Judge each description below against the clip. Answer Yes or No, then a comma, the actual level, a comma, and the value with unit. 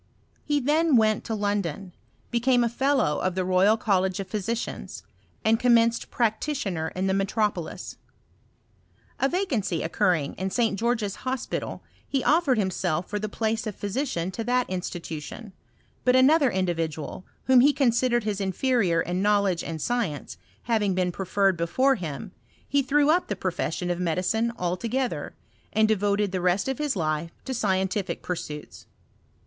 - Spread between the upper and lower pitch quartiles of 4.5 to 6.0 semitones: Yes, average, 5.0 semitones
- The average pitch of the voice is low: No, high, 205 Hz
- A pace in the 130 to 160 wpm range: Yes, average, 155 wpm